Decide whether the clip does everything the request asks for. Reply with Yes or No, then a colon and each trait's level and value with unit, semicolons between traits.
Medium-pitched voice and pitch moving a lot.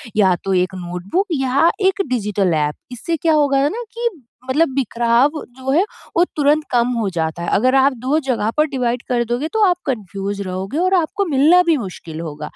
No: very high, 255 Hz; wide, 7.7 semitones